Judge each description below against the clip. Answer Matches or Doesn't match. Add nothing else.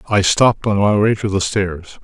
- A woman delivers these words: Doesn't match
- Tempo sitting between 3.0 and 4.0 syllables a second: Doesn't match